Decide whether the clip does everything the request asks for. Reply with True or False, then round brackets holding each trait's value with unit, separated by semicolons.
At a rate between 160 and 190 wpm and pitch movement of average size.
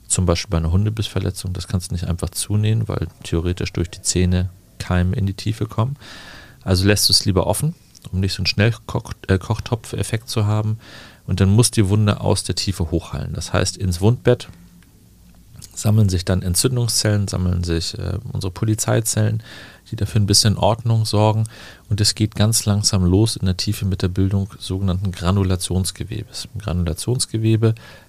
True (170 wpm; 3.1 semitones)